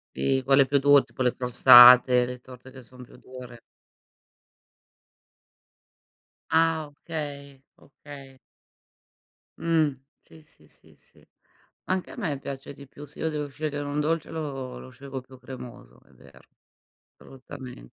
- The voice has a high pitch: No, low, 135 Hz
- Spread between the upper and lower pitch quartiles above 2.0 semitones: Yes, narrow, 2.5 semitones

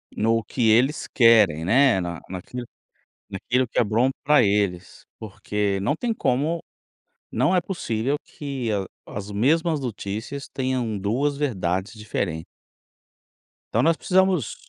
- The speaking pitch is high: No, low, 115 Hz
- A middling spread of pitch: No, wide, 5.7 semitones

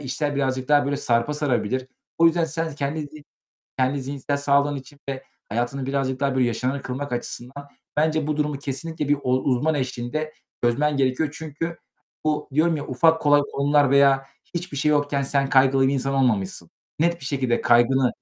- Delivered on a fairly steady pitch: Yes, narrow, 2.3 semitones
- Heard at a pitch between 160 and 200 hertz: No, medium, 140 Hz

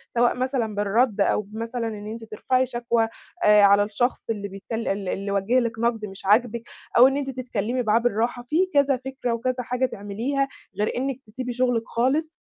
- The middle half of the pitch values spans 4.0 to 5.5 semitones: No, average, 3.3 semitones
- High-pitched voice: Yes, high, 235 Hz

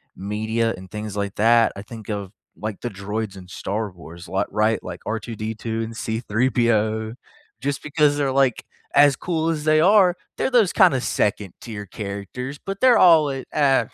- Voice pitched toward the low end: Yes, low, 115 Hz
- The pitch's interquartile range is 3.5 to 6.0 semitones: Yes, average, 5.3 semitones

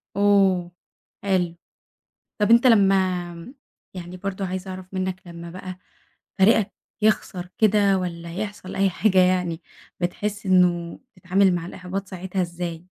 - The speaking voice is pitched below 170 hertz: No, medium, 185 Hz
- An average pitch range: No, narrow, 1.9 semitones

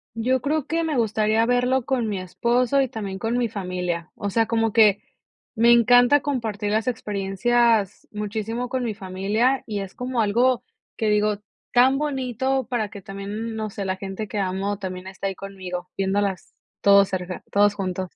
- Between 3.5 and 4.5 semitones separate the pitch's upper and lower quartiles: Yes, average, 3.8 semitones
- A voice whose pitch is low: No, high, 215 Hz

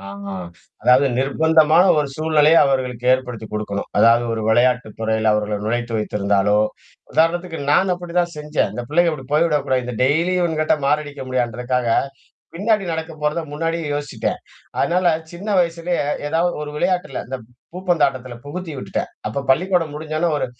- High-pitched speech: No, medium, 150 Hz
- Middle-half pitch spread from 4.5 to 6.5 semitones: Yes, average, 5.2 semitones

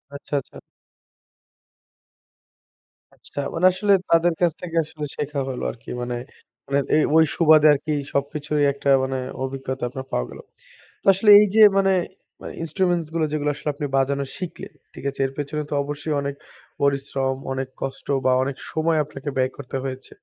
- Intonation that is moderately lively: Yes, average, 3.0 semitones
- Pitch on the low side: No, medium, 145 Hz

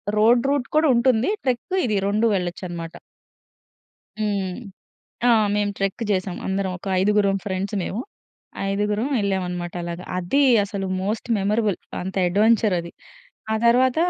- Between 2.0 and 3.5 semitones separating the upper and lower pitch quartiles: Yes, average, 3.2 semitones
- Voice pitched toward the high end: Yes, high, 200 Hz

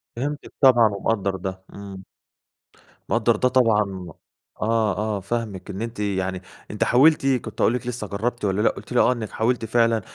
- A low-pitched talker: Yes, low, 110 Hz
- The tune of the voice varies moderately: Yes, average, 3.3 semitones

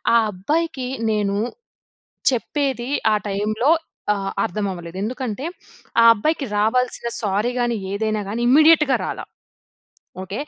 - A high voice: Yes, high, 225 Hz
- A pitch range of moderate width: Yes, average, 4.7 semitones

